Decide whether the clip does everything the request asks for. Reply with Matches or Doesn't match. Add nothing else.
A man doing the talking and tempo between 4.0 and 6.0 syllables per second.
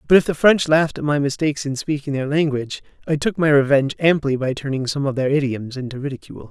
Doesn't match